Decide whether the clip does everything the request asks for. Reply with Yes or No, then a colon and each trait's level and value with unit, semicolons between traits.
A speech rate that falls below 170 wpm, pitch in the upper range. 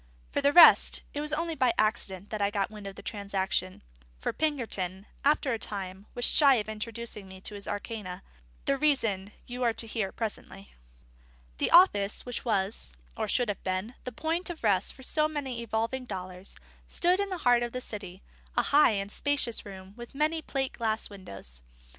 No: average, 185 wpm; high, 225 Hz